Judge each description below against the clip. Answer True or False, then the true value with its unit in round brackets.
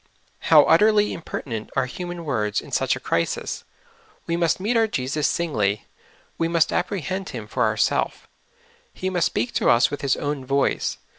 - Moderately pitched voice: True (150 Hz)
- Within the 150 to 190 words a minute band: True (170 wpm)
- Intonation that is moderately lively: False (6.1 semitones)